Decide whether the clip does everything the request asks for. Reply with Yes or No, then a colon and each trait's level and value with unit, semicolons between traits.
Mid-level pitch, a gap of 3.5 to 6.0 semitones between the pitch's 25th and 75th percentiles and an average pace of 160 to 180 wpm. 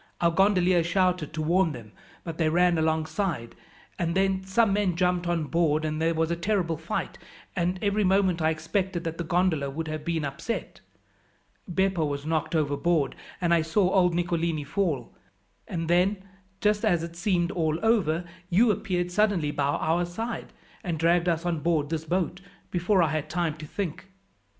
No: medium, 170 Hz; average, 2.8 semitones; average, 175 wpm